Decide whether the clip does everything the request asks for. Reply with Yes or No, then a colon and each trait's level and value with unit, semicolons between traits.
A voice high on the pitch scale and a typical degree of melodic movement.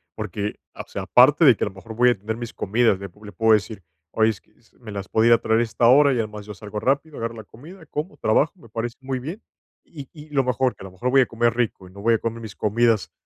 No: low, 115 Hz; average, 3.4 semitones